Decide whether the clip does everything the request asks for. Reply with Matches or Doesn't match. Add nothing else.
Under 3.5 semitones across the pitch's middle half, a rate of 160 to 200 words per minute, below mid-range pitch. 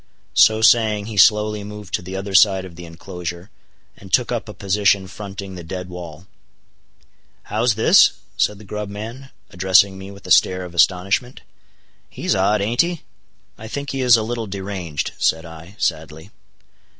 Matches